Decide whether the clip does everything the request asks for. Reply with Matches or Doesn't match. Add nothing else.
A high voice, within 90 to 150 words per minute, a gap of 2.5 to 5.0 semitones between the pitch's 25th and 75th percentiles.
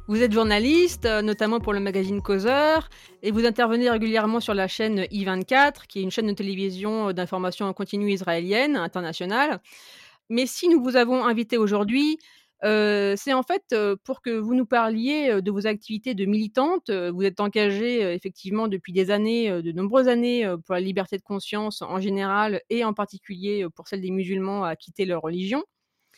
Doesn't match